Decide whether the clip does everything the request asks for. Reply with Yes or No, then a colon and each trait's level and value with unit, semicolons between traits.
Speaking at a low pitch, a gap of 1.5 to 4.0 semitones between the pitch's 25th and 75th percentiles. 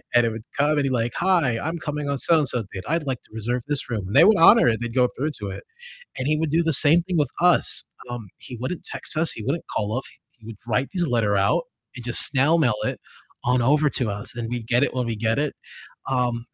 No: low, 130 Hz; average, 4.8 semitones